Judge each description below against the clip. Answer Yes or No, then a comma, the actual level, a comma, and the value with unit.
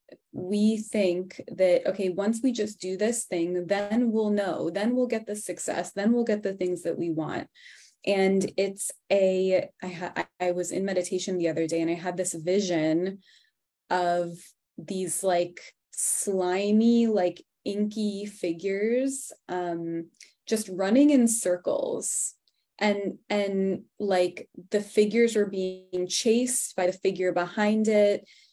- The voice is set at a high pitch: Yes, high, 195 Hz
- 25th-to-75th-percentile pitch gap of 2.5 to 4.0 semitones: Yes, average, 2.8 semitones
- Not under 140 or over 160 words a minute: Yes, average, 145 wpm